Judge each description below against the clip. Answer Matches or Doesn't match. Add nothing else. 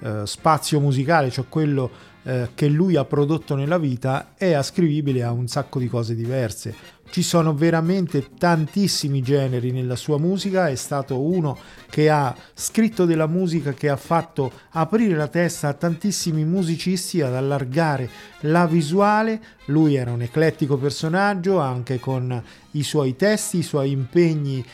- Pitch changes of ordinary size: Matches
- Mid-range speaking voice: Matches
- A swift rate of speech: Doesn't match